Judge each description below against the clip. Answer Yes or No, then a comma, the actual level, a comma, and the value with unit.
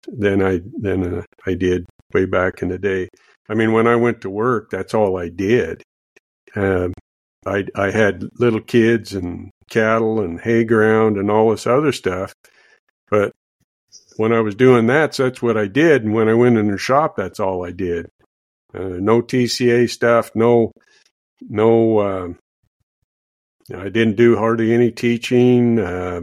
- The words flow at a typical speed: Yes, average, 180 wpm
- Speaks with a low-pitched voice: Yes, low, 110 Hz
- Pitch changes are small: No, average, 3.7 semitones